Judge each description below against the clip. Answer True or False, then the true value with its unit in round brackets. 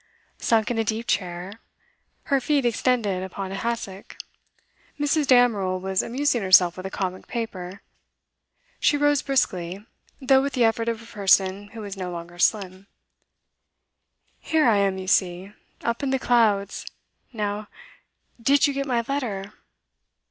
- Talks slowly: False (150 wpm)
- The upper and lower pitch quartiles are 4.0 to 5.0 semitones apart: True (4.5 semitones)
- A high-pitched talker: True (210 Hz)